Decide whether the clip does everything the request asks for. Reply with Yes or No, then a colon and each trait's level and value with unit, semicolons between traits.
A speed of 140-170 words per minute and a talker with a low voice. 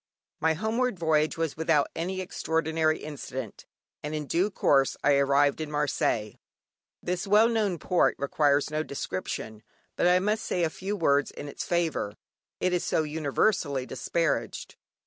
No: average, 150 wpm; medium, 160 Hz